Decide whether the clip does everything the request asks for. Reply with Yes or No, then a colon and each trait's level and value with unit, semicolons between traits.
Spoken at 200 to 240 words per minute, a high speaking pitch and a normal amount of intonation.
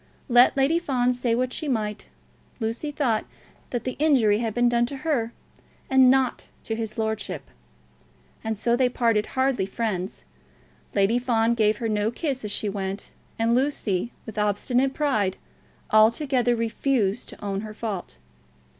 No: average, 155 wpm; high, 230 Hz; average, 3.2 semitones